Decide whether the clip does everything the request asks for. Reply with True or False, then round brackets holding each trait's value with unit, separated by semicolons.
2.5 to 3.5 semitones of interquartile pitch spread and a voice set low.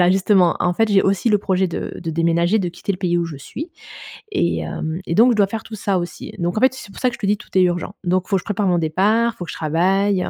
False (3.1 semitones; 185 Hz)